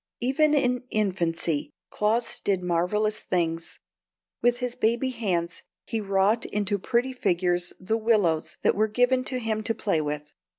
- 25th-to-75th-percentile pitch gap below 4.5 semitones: No, average, 5.1 semitones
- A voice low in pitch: No, high, 210 Hz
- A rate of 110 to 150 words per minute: Yes, average, 140 wpm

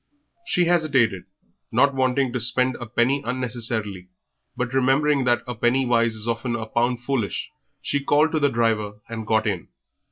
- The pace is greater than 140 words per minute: Yes, average, 165 wpm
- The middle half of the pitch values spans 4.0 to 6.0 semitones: No, average, 2.9 semitones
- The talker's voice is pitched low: Yes, low, 120 Hz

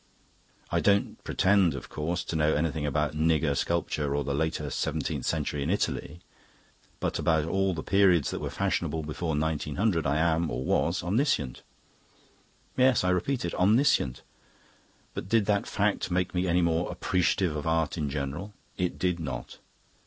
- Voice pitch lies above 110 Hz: No, very low, 85 Hz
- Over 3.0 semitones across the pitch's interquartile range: Yes, average, 3.5 semitones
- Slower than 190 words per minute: Yes, average, 160 wpm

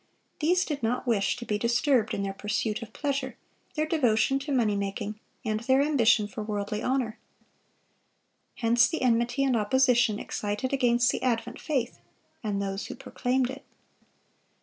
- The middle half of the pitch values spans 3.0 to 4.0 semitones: Yes, average, 3.7 semitones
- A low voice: No, high, 240 Hz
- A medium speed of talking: Yes, average, 155 wpm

